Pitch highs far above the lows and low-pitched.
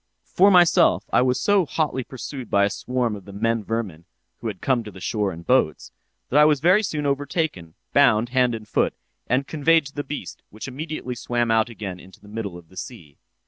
Yes: wide, 5.8 semitones; low, 120 Hz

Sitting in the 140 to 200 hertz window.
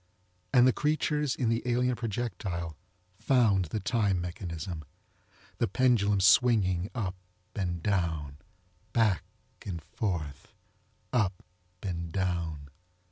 No: very low, 95 Hz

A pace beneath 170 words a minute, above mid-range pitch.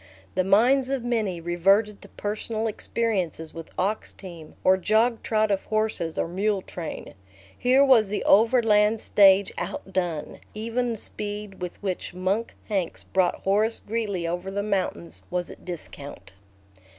Yes: average, 140 wpm; high, 200 Hz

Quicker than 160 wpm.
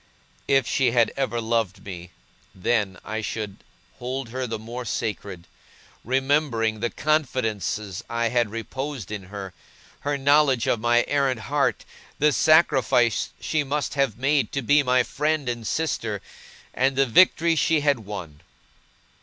No: average, 145 wpm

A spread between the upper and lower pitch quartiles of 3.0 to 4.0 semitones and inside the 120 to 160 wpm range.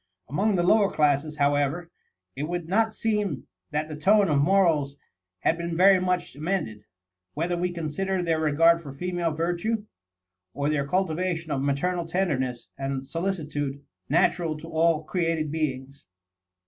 Yes: average, 3.7 semitones; average, 145 wpm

